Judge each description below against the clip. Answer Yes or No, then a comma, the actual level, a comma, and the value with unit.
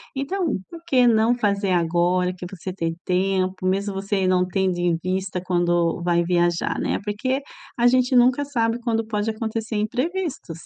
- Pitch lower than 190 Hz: No, high, 195 Hz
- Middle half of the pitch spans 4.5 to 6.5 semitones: Yes, average, 4.8 semitones